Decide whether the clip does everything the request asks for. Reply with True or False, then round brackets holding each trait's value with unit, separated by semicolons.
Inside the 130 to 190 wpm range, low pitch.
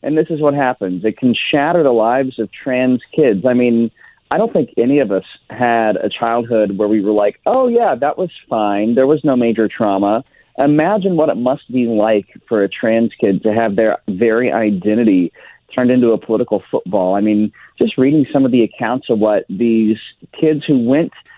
False (200 wpm; 120 Hz)